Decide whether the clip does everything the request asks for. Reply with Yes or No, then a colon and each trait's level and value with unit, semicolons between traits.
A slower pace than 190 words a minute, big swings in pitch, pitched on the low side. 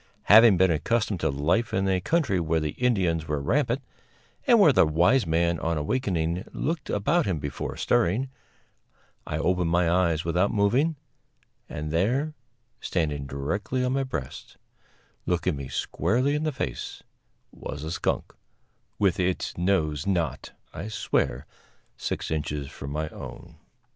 Yes: average, 145 wpm; wide, 6.9 semitones; very low, 90 Hz